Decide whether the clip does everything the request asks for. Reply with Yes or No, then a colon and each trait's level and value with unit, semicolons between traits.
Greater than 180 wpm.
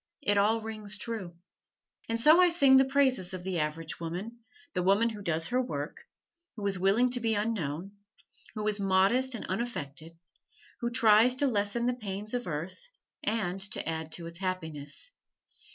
No: average, 170 wpm